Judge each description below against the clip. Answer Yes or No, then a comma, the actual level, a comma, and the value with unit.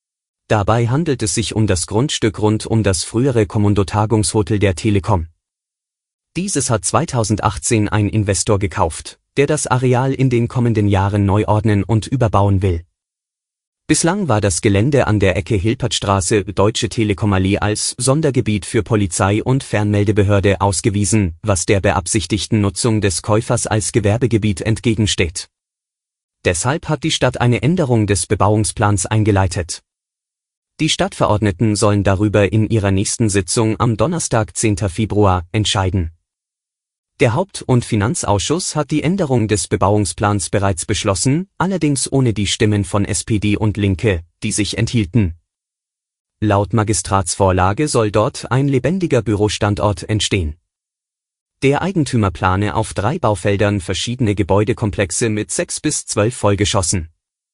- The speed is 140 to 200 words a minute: No, average, 130 wpm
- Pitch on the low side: Yes, low, 105 Hz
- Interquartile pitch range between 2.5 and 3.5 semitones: Yes, average, 2.8 semitones